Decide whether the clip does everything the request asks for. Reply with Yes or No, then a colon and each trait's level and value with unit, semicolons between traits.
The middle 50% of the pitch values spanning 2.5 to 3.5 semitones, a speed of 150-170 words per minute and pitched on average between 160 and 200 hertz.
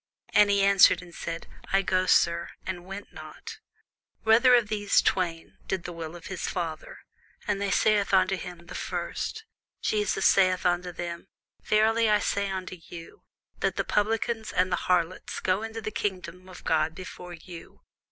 Yes: average, 2.8 semitones; average, 165 wpm; medium, 185 Hz